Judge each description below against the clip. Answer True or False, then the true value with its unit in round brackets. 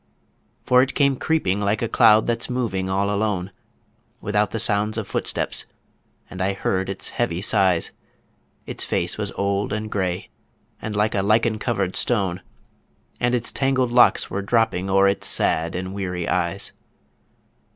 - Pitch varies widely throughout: False (3.1 semitones)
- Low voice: True (100 Hz)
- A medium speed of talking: True (155 wpm)